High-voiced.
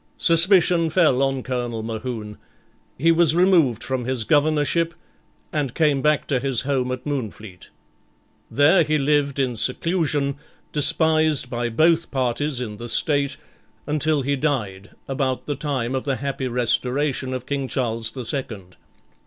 No: low, 135 Hz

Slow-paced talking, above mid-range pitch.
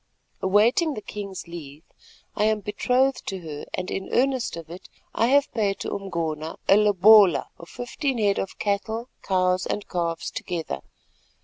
No: average, 155 wpm; high, 200 Hz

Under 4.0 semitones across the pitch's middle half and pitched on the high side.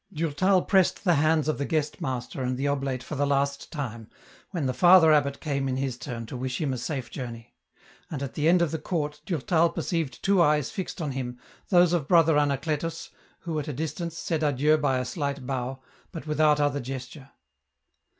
No: average, 3.5 semitones; medium, 145 Hz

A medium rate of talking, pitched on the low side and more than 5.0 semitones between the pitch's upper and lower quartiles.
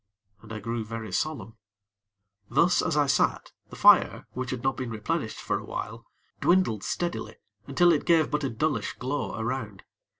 Yes: average, 170 wpm; low, 130 Hz; wide, 5.5 semitones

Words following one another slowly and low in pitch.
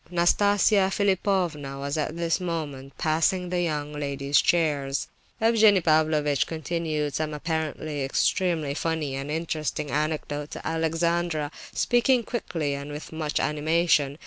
No: slow, 120 wpm; medium, 155 Hz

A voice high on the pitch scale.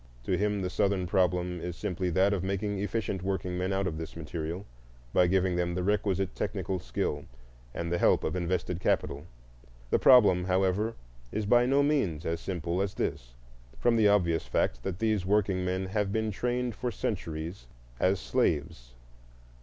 No: very low, 95 Hz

